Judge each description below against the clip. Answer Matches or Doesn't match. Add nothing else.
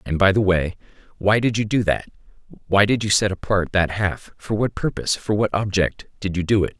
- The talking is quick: Matches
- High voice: Doesn't match